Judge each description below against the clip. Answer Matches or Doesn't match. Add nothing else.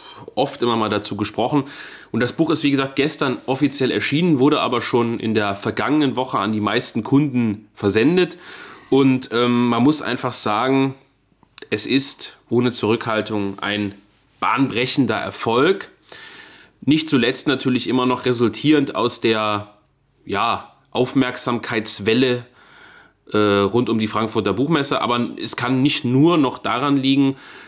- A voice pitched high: Doesn't match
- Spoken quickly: Doesn't match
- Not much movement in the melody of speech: Doesn't match